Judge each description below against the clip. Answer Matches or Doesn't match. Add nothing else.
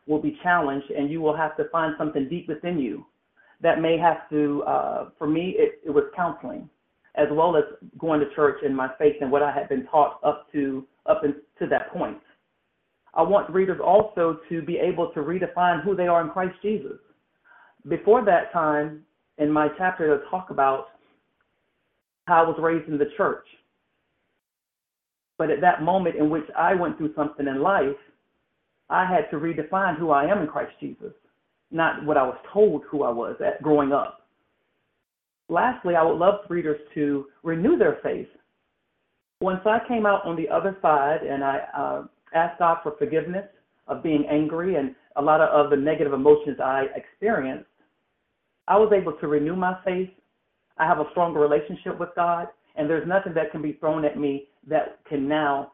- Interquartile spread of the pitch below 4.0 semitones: Matches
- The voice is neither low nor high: Matches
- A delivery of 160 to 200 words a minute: Matches